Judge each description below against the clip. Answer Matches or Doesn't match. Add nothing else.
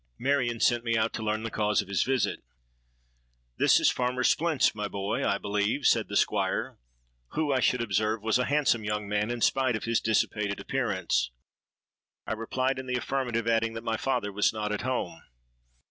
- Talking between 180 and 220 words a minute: Matches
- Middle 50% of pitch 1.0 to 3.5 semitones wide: Matches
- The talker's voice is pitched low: Matches